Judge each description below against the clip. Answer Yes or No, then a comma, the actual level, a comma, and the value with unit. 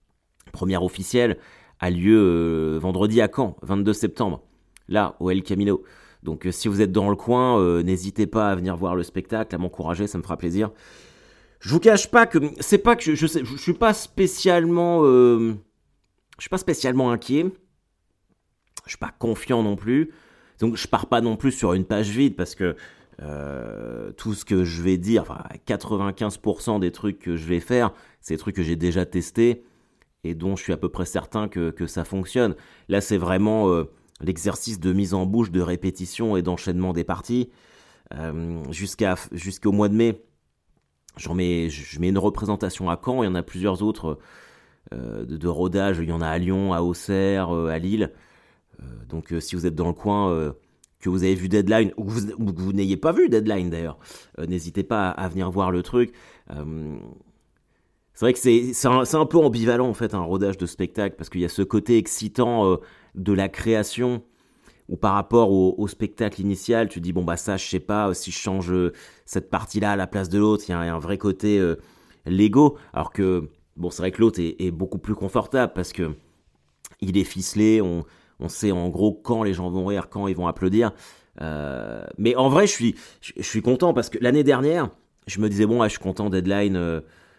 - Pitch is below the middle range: Yes, low, 100 Hz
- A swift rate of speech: No, average, 210 wpm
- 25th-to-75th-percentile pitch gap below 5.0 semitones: Yes, average, 4.1 semitones